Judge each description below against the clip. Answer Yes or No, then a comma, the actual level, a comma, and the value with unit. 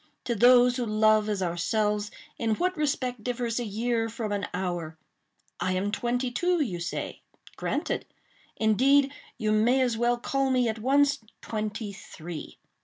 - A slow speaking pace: No, average, 155 wpm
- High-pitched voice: Yes, high, 225 Hz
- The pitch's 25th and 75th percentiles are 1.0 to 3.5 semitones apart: Yes, average, 3.2 semitones